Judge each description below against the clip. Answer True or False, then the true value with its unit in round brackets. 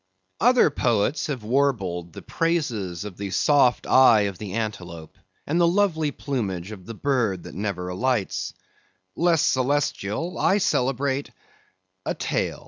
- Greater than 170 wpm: False (135 wpm)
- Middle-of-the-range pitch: False (120 Hz)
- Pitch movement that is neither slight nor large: False (6.8 semitones)